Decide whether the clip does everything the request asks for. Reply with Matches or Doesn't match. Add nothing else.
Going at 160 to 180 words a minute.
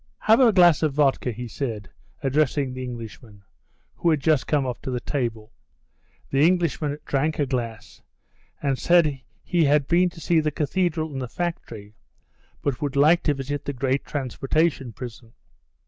Matches